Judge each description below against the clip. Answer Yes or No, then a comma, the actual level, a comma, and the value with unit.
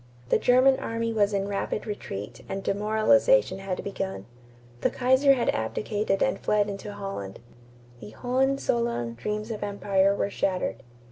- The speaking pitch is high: Yes, high, 205 Hz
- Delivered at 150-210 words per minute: No, average, 140 wpm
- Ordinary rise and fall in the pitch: Yes, average, 3.4 semitones